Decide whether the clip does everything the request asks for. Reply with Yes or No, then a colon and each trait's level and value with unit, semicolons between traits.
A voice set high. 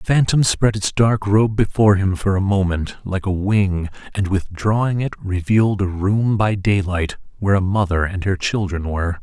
No: low, 100 Hz